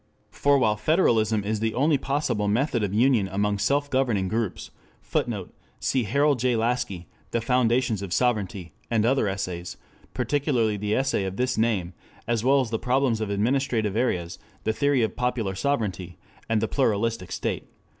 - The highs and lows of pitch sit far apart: No, average, 4.0 semitones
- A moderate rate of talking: Yes, average, 165 wpm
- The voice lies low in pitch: Yes, low, 115 Hz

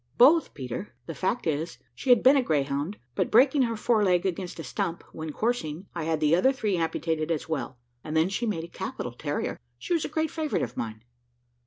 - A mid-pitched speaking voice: Yes, medium, 170 Hz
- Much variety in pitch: Yes, wide, 7.4 semitones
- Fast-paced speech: Yes, fast, 215 wpm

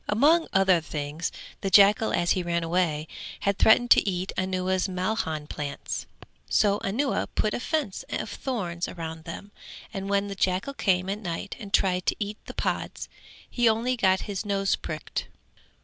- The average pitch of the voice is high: Yes, high, 195 Hz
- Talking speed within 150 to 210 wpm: Yes, average, 165 wpm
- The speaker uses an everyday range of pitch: Yes, average, 3.2 semitones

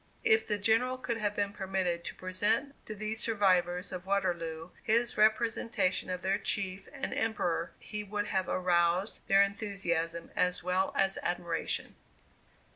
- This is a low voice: No, high, 195 Hz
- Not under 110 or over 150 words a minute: Yes, average, 145 wpm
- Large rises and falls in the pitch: No, average, 3.1 semitones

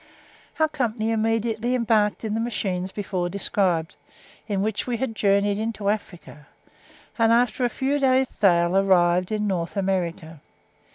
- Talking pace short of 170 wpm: Yes, average, 140 wpm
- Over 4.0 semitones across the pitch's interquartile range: No, average, 3.5 semitones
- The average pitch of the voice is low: No, high, 210 Hz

